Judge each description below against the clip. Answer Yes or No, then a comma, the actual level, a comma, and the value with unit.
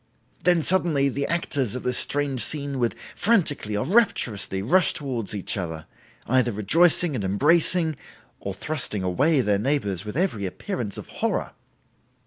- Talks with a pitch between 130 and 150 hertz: Yes, low, 135 Hz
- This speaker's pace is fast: No, average, 145 wpm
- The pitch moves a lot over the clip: Yes, wide, 7.5 semitones